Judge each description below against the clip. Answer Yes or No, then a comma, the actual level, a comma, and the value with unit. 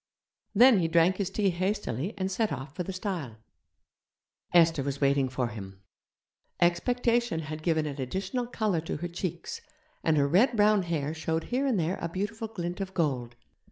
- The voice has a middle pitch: Yes, medium, 175 Hz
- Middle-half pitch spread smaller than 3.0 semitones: No, average, 5.1 semitones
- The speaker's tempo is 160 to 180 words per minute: Yes, average, 175 wpm